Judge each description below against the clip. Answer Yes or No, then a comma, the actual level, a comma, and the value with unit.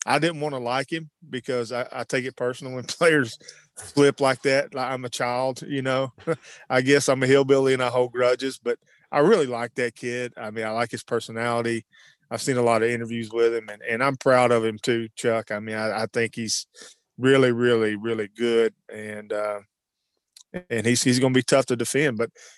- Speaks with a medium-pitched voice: No, low, 125 Hz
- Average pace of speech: No, fast, 220 wpm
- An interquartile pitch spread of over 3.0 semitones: No, narrow, 2.5 semitones